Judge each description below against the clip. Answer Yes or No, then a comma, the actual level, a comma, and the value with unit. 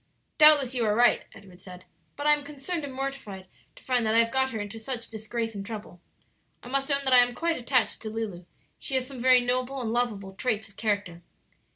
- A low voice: No, high, 240 Hz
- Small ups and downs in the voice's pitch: No, average, 3.7 semitones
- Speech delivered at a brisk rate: Yes, fast, 220 wpm